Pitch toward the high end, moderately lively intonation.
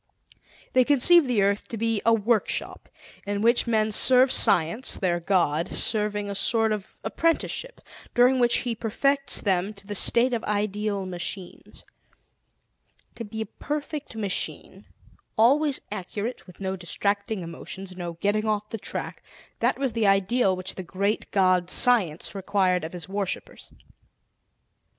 Yes: high, 210 Hz; average, 3.8 semitones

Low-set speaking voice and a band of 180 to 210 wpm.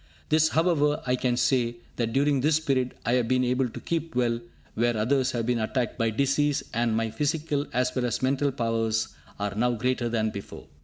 Yes: low, 125 Hz; average, 200 wpm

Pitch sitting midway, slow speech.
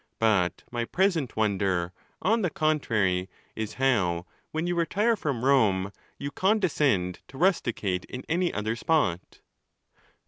No: low, 125 Hz; slow, 130 wpm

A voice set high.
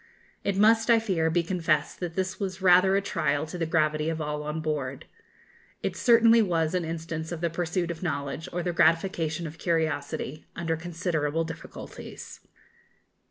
No: medium, 165 Hz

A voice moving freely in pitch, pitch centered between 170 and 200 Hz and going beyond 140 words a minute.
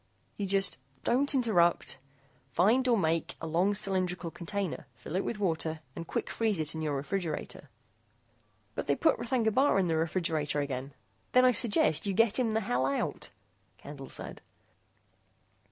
Yes: wide, 5.7 semitones; medium, 185 Hz; average, 170 wpm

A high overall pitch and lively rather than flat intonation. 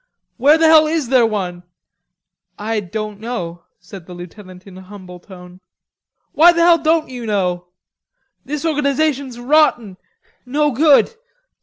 Yes: high, 230 Hz; wide, 8.2 semitones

